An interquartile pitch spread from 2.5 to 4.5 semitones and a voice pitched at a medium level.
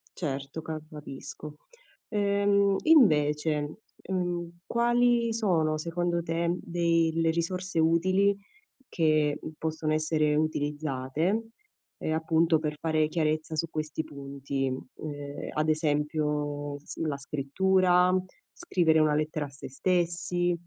Yes: average, 2.8 semitones; medium, 160 Hz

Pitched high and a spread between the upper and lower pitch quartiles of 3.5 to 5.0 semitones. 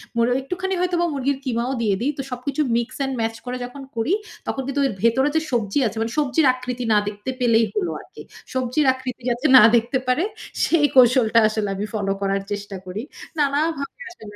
Yes: very high, 250 Hz; average, 3.8 semitones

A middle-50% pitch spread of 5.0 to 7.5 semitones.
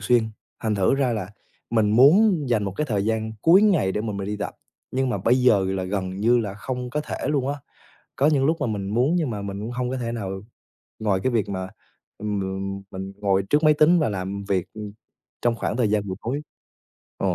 No: average, 4.6 semitones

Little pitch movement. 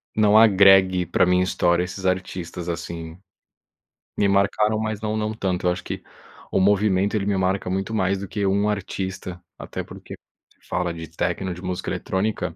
Yes: narrow, 2.1 semitones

